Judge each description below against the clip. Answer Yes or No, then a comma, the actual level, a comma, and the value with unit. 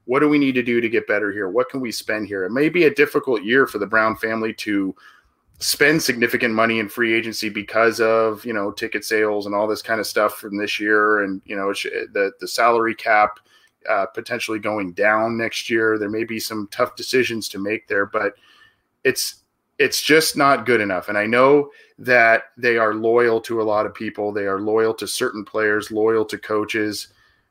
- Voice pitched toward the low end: Yes, low, 110 Hz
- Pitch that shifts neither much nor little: No, narrow, 1.9 semitones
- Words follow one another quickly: Yes, fast, 210 wpm